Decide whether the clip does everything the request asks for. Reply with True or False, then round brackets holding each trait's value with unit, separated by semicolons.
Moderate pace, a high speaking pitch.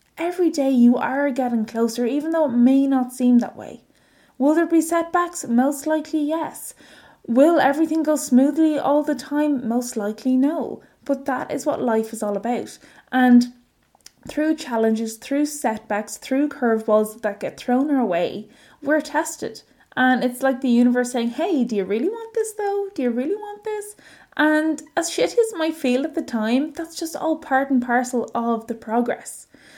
True (180 wpm; 270 Hz)